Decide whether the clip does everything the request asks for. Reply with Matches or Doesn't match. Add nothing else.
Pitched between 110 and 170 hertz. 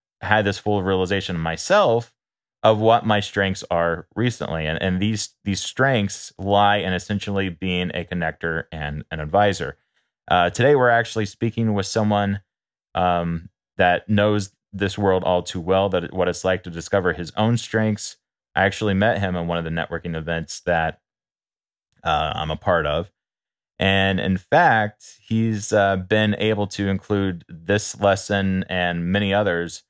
Doesn't match